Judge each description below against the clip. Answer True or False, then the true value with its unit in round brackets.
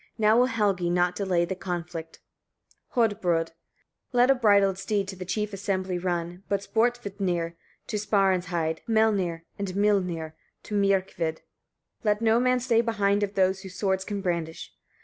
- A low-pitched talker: False (195 Hz)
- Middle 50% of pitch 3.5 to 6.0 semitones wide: False (3.0 semitones)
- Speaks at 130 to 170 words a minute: True (150 wpm)